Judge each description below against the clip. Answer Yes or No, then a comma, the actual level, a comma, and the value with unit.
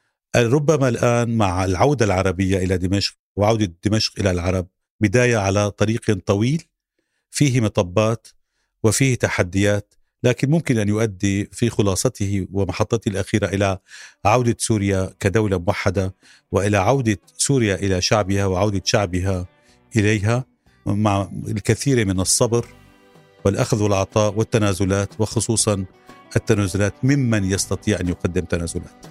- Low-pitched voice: Yes, low, 105 Hz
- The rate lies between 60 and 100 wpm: No, average, 110 wpm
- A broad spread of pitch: No, average, 2.9 semitones